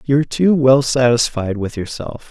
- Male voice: Yes, male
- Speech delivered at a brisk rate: No, average, 155 wpm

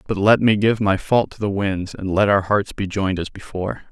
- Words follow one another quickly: Yes, fast, 260 wpm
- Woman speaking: No, male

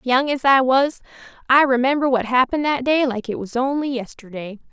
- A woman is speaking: Yes, female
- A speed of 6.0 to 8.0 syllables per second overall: No, 5.5 syllables/s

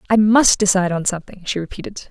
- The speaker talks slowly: No, average, 200 wpm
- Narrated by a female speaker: Yes, female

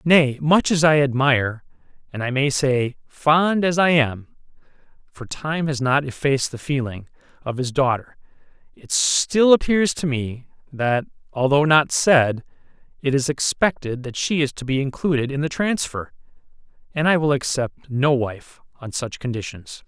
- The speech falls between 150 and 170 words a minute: Yes, average, 160 wpm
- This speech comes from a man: Yes, male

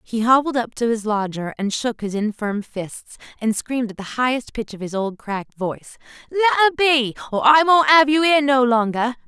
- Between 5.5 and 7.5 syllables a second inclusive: No, 5.3 syllables/s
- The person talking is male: No, female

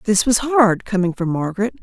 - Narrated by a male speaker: No, female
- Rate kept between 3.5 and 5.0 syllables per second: No, 5.6 syllables/s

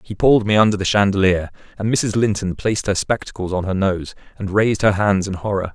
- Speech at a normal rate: No, fast, 220 wpm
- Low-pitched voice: Yes, low, 100 Hz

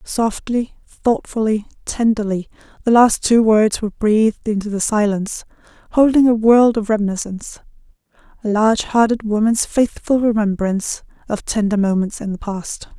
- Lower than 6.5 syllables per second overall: Yes, 5.0 syllables/s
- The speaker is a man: No, female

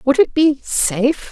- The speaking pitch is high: Yes, very high, 270 Hz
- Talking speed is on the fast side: No, slow, 135 wpm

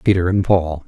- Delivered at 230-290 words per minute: No, fast, 205 wpm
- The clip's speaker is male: Yes, male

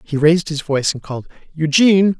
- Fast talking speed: No, average, 190 wpm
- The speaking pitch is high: No, medium, 160 Hz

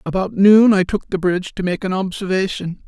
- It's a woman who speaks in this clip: No, male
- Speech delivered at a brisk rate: Yes, fast, 210 wpm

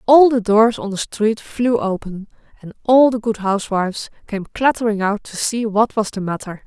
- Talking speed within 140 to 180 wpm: No, average, 200 wpm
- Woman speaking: Yes, female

